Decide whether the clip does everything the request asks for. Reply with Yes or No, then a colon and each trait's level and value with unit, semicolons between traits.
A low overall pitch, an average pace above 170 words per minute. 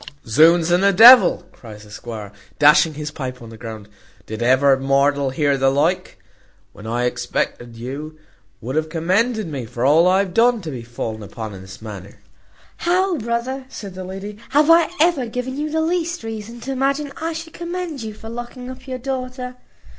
No: medium, 180 Hz; average, 190 wpm